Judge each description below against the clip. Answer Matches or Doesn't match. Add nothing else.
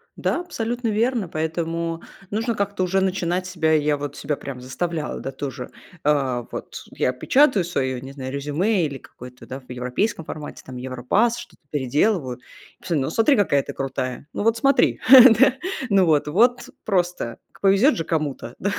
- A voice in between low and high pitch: Matches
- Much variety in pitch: Matches